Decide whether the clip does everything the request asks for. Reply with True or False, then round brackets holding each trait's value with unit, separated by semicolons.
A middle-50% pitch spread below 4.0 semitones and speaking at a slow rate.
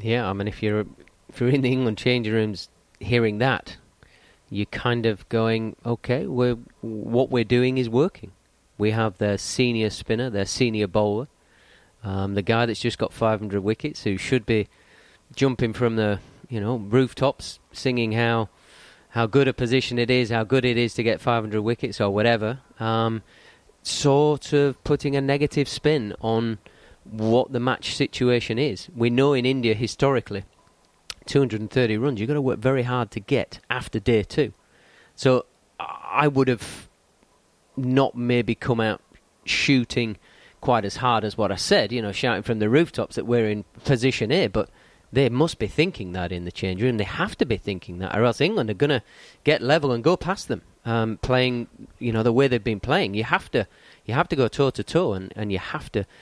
False (3.3 semitones; 190 wpm)